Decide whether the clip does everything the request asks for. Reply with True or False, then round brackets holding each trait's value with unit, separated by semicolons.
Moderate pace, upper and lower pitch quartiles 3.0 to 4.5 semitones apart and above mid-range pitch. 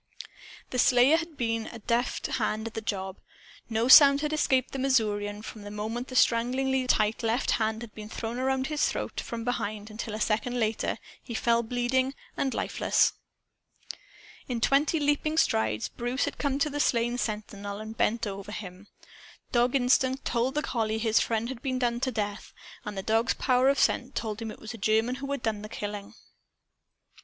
True (185 wpm; 3.3 semitones; 235 Hz)